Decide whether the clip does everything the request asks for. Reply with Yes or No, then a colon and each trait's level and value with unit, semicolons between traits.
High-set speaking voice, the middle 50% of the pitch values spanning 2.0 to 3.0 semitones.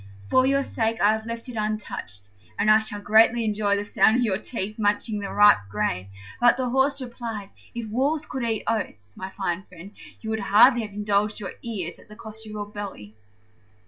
Yes: high, 215 Hz; narrow, 2.4 semitones